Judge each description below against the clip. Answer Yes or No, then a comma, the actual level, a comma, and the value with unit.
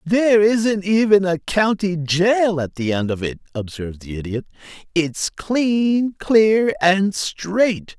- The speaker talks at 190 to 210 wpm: No, average, 145 wpm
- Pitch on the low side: No, medium, 185 Hz